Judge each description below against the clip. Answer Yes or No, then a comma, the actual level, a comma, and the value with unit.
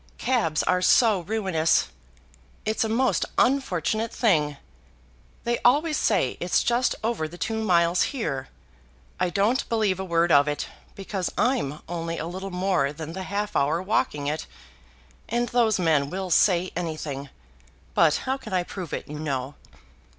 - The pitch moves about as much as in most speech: No, wide, 5.8 semitones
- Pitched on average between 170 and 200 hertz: Yes, medium, 185 Hz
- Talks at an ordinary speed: Yes, average, 155 wpm